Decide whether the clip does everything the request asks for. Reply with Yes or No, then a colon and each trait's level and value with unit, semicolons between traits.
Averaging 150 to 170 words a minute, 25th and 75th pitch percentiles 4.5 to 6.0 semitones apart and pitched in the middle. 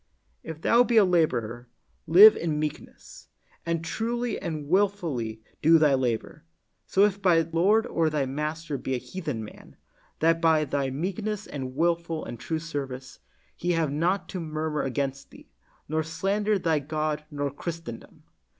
No: average, 155 wpm; average, 3.7 semitones; medium, 160 Hz